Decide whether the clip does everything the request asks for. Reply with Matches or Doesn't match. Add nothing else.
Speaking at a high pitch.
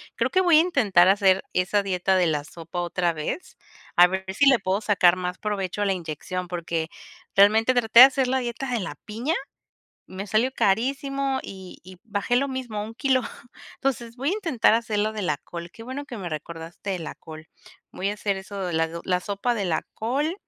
Matches